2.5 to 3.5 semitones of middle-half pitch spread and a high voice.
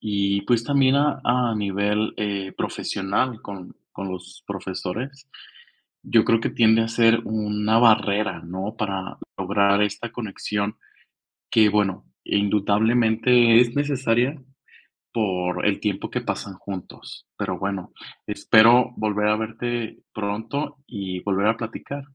No: average, 2.8 semitones; low, 110 Hz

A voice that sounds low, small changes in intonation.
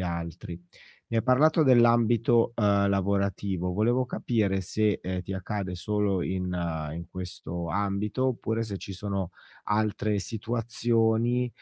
No: low, 100 Hz; average, 3.9 semitones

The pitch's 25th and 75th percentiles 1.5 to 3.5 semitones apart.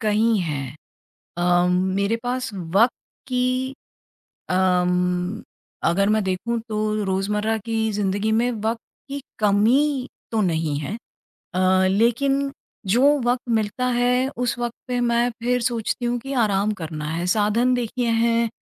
No: average, 4.4 semitones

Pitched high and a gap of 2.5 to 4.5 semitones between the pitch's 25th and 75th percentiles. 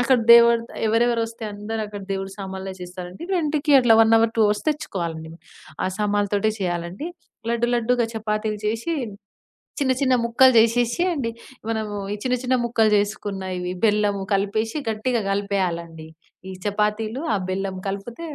Yes: high, 215 Hz; average, 3.0 semitones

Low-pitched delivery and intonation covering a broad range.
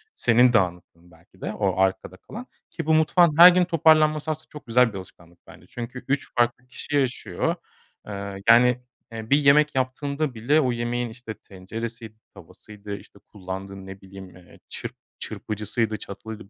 Yes: low, 115 Hz; wide, 6.3 semitones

